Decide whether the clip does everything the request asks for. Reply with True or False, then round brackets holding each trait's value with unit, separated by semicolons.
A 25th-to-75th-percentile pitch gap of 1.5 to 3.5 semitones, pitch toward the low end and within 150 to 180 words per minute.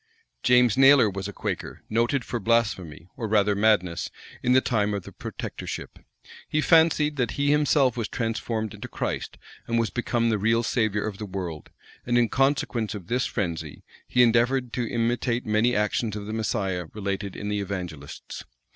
True (3.2 semitones; 115 Hz; 175 wpm)